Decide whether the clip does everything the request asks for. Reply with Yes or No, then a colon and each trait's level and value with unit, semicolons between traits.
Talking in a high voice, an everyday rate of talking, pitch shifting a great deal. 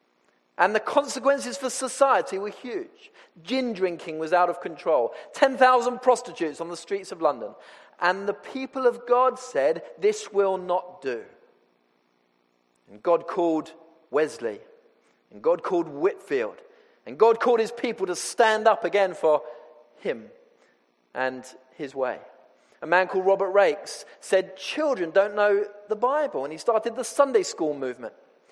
Yes: high, 200 Hz; average, 145 wpm; wide, 8.6 semitones